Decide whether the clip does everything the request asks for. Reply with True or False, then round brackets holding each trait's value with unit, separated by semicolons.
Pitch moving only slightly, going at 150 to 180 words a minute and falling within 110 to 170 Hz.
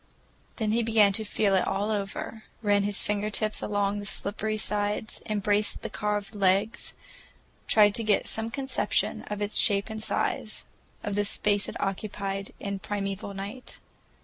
False (1.3 semitones; 160 wpm; 205 Hz)